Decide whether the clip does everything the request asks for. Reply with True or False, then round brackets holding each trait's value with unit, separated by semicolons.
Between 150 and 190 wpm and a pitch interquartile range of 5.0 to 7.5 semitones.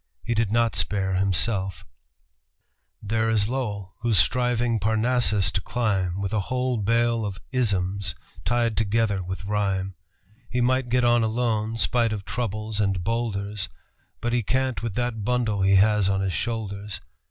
False (155 wpm; 3.2 semitones)